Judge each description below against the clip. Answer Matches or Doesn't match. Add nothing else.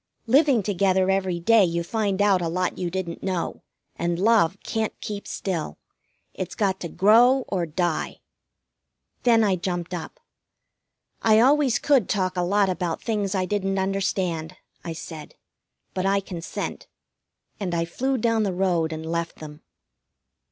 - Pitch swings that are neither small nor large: Matches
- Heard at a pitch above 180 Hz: Matches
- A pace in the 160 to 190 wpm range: Doesn't match